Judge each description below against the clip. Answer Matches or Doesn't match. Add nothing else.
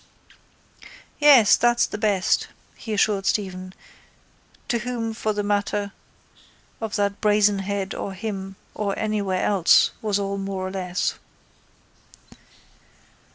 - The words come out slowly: Matches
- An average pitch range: Doesn't match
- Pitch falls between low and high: Doesn't match